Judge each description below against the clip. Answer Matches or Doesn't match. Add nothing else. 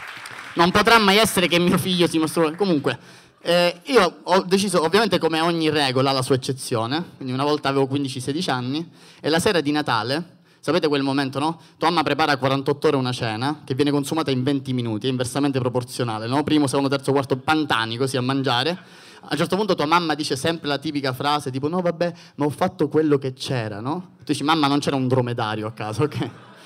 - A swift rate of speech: Matches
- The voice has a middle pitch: Matches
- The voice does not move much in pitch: Doesn't match